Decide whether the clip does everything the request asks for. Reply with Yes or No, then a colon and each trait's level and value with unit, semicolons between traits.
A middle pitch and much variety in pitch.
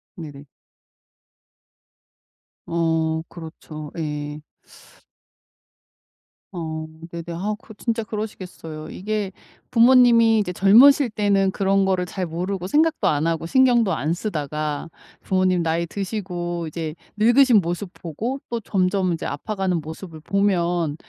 No: medium, 180 Hz; average, 4.6 semitones